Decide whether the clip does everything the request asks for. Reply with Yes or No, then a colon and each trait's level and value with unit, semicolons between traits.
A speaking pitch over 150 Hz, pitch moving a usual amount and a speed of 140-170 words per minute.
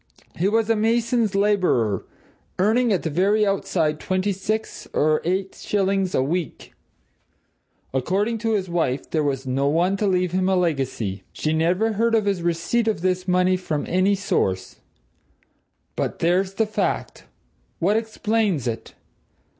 Yes: medium, 185 Hz; average, 4.3 semitones; average, 150 wpm